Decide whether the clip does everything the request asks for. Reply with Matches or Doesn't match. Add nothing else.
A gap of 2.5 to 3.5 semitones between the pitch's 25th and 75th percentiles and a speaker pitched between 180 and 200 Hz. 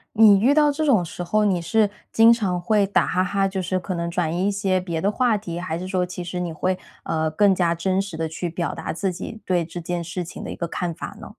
Matches